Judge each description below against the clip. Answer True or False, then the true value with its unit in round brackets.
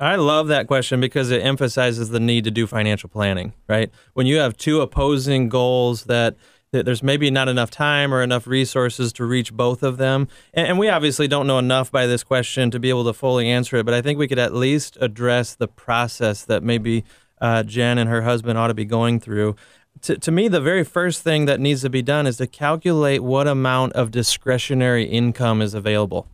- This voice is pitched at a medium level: False (125 Hz)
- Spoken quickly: True (220 wpm)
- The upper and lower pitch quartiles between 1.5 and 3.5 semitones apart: True (2.8 semitones)